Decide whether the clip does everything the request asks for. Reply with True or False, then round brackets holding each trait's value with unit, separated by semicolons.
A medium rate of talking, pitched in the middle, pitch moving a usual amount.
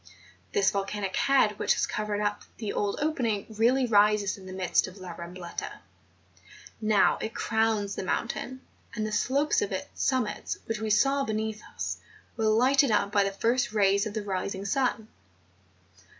False (165 wpm; 215 Hz; 3.0 semitones)